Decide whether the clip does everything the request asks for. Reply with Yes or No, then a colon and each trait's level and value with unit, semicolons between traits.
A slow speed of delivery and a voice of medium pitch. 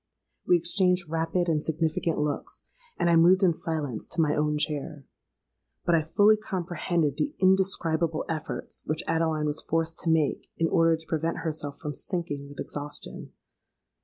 No: average, 160 wpm; medium, 165 Hz